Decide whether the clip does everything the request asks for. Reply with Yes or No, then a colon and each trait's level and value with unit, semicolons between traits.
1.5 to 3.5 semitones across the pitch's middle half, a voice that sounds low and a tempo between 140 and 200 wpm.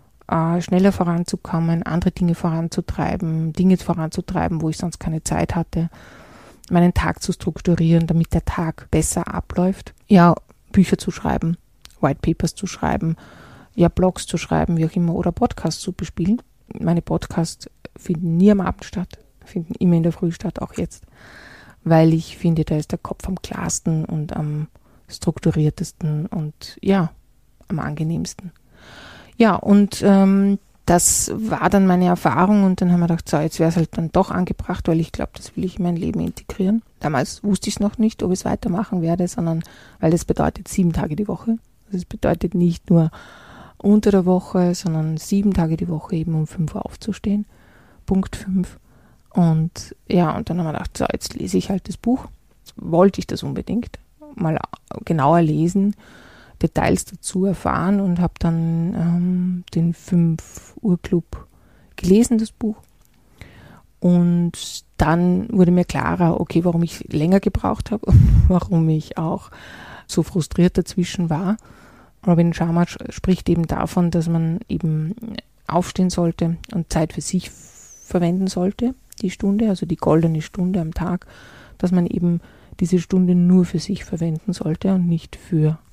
No: narrow, 2.4 semitones; medium, 175 Hz; average, 160 wpm